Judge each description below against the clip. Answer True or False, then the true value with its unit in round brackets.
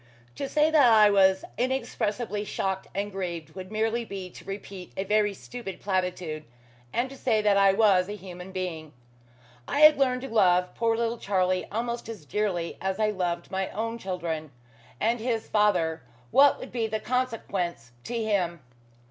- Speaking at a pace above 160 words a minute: True (170 wpm)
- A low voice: False (205 Hz)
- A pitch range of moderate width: True (3.7 semitones)